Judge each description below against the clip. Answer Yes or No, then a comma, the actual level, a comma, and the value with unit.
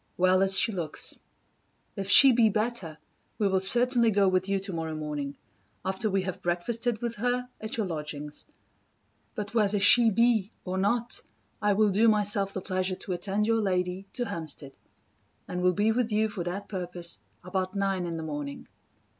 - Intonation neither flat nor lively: Yes, average, 3.3 semitones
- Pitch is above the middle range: Yes, high, 195 Hz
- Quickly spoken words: No, average, 175 wpm